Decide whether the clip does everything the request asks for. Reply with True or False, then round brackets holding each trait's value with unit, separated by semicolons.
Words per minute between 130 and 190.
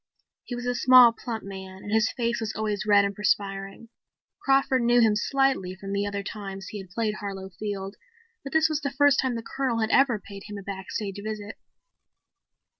False (200 wpm)